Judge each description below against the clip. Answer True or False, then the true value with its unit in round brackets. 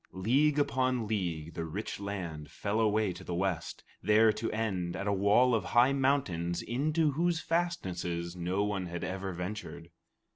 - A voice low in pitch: True (100 Hz)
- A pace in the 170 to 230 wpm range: False (160 wpm)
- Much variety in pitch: True (6.1 semitones)